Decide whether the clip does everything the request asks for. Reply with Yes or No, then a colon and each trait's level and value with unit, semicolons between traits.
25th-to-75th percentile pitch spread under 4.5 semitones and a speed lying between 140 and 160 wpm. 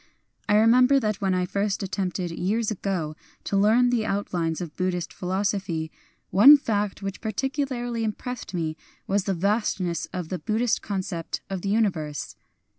Yes: average, 3.5 semitones; average, 155 wpm